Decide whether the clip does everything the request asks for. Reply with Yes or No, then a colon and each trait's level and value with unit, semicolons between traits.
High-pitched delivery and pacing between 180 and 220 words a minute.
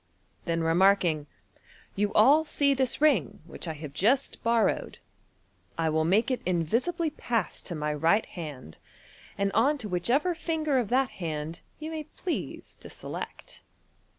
No: high, 205 Hz; average, 155 wpm